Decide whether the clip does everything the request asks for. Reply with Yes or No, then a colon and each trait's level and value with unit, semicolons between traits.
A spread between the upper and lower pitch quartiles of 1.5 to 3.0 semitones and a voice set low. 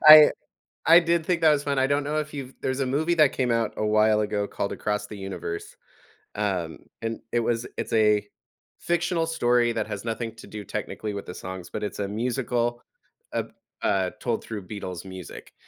No: average, 5.2 semitones; low, 115 Hz